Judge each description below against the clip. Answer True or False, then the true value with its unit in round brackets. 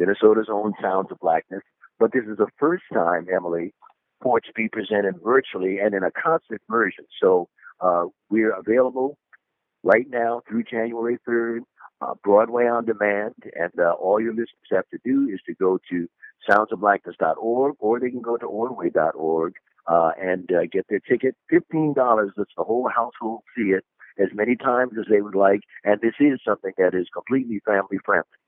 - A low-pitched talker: True (110 Hz)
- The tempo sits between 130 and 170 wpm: False (180 wpm)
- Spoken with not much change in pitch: False (4.1 semitones)